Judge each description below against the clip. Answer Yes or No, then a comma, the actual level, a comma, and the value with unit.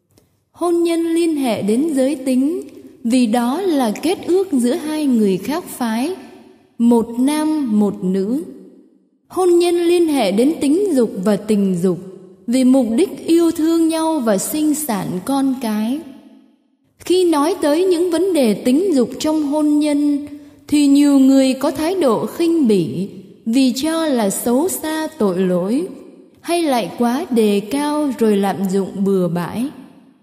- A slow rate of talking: Yes, slow, 155 wpm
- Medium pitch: No, very high, 270 Hz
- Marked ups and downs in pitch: Yes, wide, 5.7 semitones